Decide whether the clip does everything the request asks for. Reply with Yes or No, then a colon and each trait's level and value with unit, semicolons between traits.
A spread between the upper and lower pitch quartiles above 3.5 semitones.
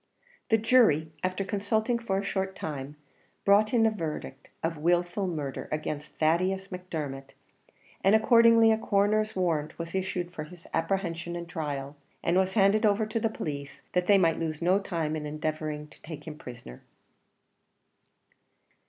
Yes: average, 4.5 semitones